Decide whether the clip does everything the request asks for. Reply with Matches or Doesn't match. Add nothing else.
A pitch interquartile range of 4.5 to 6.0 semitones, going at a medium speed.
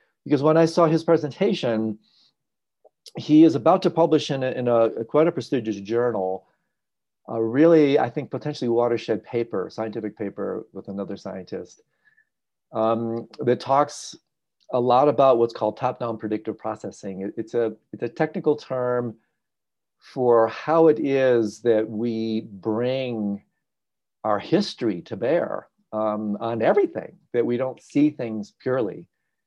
Matches